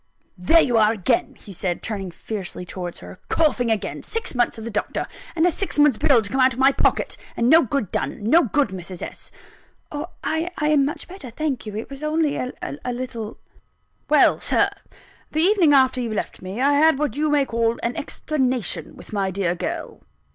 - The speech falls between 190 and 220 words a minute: Yes, average, 200 wpm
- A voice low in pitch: No, very high, 255 Hz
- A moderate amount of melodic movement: No, wide, 6.0 semitones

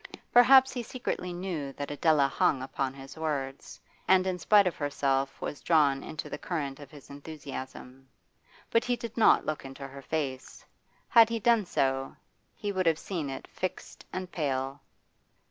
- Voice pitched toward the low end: No, medium, 150 Hz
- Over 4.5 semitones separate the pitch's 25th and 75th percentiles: Yes, wide, 5.4 semitones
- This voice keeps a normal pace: Yes, average, 165 wpm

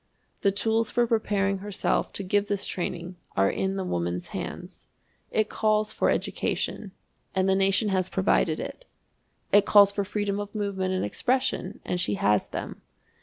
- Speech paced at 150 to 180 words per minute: Yes, average, 165 wpm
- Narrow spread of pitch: Yes, narrow, 1.9 semitones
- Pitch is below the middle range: No, high, 195 Hz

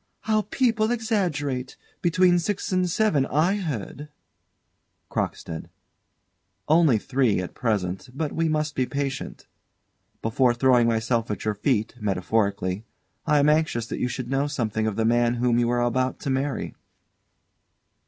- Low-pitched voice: Yes, low, 130 Hz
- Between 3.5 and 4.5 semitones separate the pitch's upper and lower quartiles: No, wide, 5.5 semitones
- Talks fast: No, average, 145 wpm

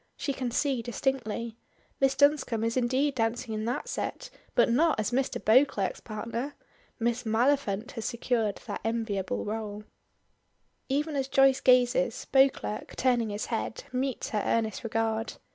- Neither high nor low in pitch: No, high, 235 Hz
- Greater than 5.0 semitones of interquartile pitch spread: No, average, 3.2 semitones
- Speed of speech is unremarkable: Yes, average, 145 wpm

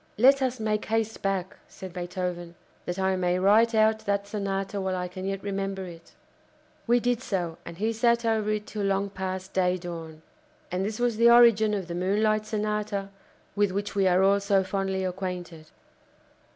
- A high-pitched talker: Yes, high, 195 Hz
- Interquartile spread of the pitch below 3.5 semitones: Yes, narrow, 2.6 semitones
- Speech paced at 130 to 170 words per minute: No, average, 180 wpm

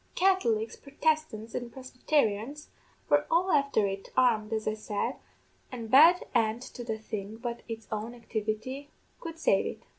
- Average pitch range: Yes, average, 4.7 semitones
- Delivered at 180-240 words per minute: No, average, 150 wpm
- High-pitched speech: Yes, high, 235 Hz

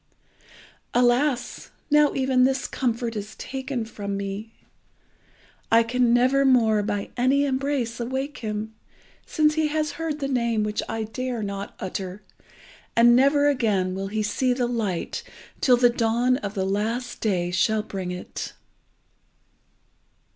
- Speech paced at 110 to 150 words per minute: Yes, average, 140 wpm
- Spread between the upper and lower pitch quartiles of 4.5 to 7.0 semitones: No, average, 3.8 semitones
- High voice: Yes, high, 235 Hz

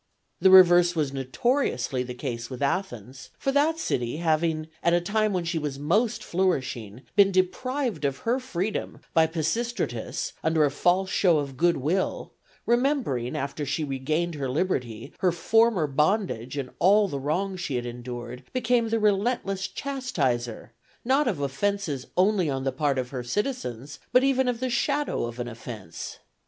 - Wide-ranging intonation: Yes, wide, 7.8 semitones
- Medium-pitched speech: Yes, medium, 165 Hz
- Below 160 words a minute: No, average, 165 wpm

